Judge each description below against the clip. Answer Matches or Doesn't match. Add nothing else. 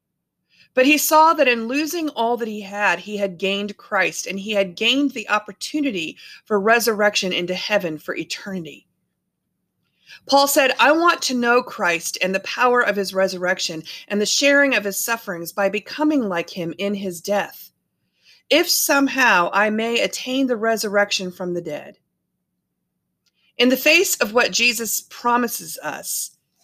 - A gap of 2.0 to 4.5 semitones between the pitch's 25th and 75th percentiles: Doesn't match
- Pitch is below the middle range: Doesn't match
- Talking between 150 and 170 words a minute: Matches